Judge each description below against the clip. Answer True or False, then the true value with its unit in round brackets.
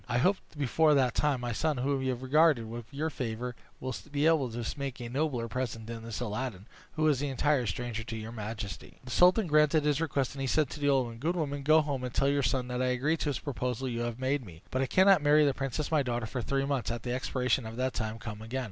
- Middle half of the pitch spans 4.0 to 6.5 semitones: False (3.5 semitones)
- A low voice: True (130 Hz)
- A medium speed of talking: False (265 wpm)